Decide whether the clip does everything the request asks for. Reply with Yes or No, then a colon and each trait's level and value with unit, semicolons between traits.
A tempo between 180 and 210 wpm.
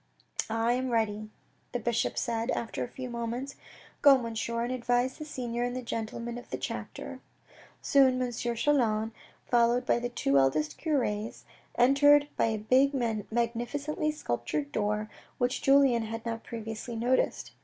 No: average, 155 wpm